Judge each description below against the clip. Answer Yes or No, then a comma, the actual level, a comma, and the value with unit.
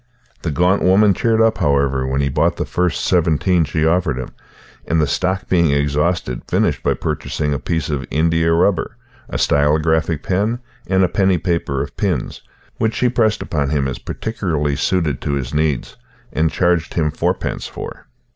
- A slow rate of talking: No, average, 175 wpm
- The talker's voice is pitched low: Yes, very low, 80 Hz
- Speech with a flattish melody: No, average, 4.1 semitones